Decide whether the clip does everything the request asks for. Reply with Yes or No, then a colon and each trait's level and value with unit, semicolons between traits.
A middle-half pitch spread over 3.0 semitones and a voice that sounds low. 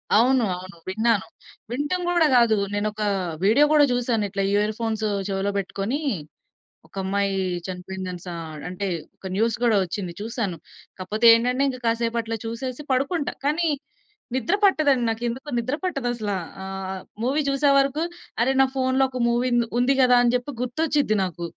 No: average, 4.8 semitones; high, 235 Hz